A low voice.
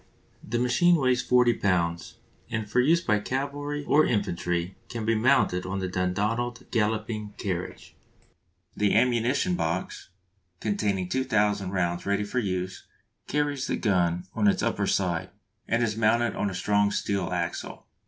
Yes: low, 105 Hz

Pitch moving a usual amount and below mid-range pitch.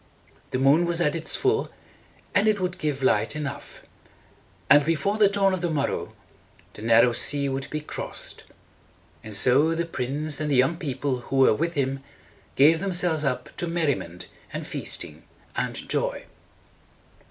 No: average, 4.1 semitones; medium, 150 Hz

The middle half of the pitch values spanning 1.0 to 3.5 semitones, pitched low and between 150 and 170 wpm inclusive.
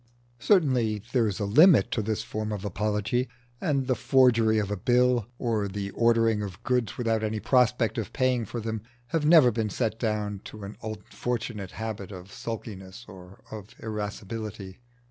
Yes: average, 2.8 semitones; low, 110 Hz; average, 165 wpm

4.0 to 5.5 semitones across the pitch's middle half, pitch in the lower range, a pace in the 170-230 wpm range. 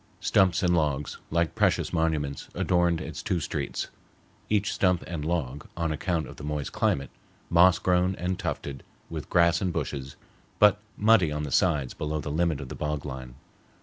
No: average, 3.4 semitones; very low, 80 Hz; average, 175 wpm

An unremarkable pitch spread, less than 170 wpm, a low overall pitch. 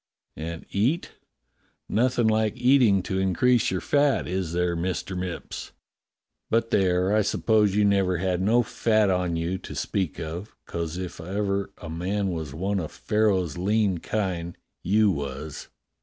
Yes: average, 3.5 semitones; average, 150 wpm; very low, 95 Hz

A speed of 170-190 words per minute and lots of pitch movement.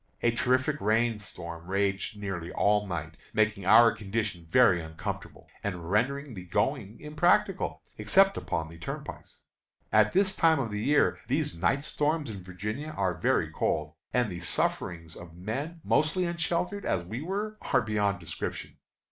No: average, 155 wpm; wide, 8.4 semitones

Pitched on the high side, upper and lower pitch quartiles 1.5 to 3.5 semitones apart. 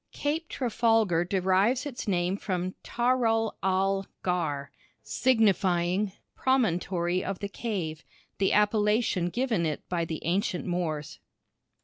No: high, 195 Hz; average, 4.3 semitones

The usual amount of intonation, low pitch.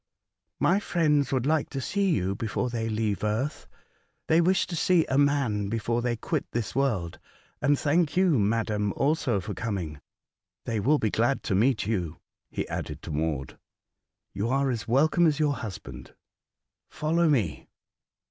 No: wide, 6.1 semitones; low, 120 Hz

